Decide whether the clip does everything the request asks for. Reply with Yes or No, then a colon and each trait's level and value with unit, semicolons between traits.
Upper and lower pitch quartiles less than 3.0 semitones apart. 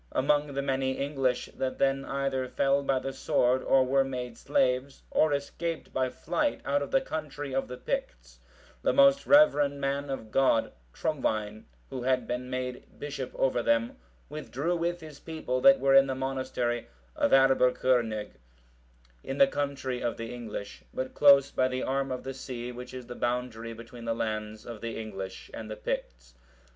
Yes: narrow, 2.4 semitones